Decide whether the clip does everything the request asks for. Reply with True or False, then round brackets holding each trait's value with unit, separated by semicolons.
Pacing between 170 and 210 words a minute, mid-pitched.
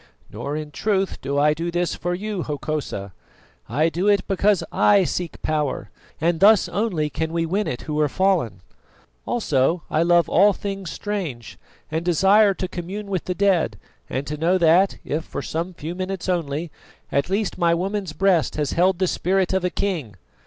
True (180 wpm; 175 Hz)